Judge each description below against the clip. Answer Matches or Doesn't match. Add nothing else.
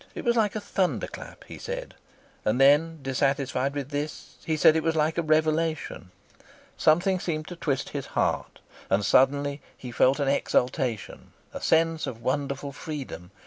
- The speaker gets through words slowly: Doesn't match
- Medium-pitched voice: Matches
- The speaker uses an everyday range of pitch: Matches